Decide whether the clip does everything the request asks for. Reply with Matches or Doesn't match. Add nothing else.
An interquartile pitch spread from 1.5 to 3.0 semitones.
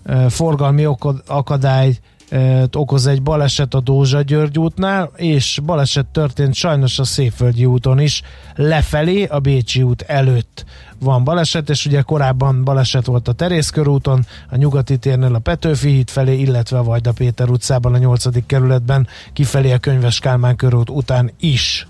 Matches